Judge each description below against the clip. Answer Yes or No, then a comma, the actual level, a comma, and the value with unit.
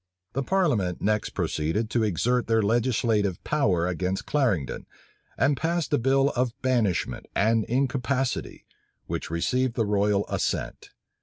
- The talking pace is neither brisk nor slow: No, slow, 130 wpm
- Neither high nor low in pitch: No, low, 115 Hz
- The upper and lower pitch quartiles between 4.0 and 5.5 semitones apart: Yes, average, 4.5 semitones